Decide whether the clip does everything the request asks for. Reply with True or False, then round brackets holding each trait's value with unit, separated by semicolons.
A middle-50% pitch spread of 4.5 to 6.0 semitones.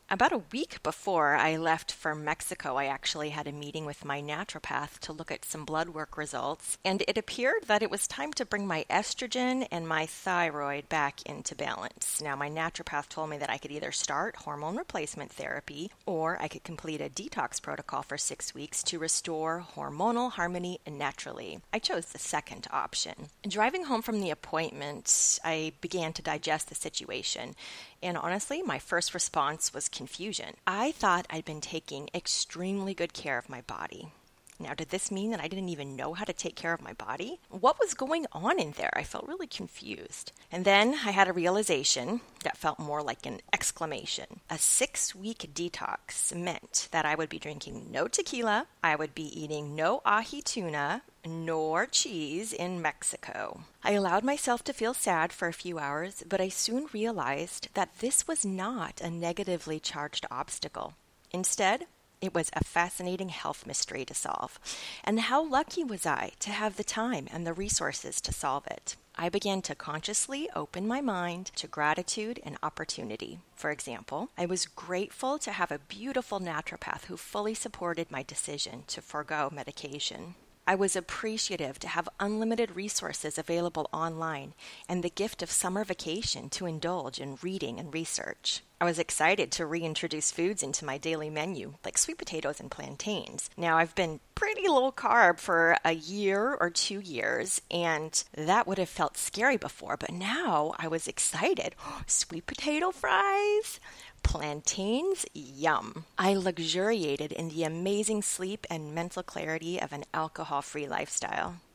True (4.8 semitones)